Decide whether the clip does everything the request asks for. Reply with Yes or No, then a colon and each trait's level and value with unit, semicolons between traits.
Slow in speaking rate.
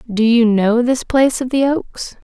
No: fast, 205 wpm